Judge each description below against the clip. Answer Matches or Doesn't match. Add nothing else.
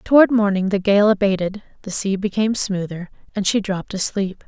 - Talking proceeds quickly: Doesn't match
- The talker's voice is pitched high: Matches